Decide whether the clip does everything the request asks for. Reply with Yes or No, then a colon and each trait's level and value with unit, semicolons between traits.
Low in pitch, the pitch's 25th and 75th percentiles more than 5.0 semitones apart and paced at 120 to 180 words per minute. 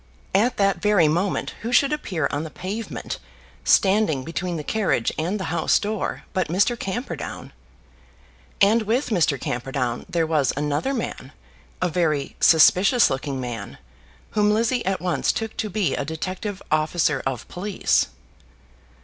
No: medium, 180 Hz; wide, 5.5 semitones; average, 145 wpm